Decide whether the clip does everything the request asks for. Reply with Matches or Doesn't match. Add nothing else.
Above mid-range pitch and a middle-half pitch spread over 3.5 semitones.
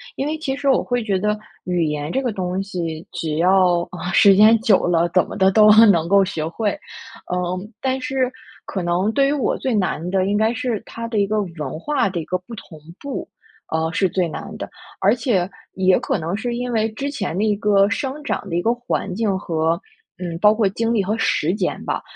Matches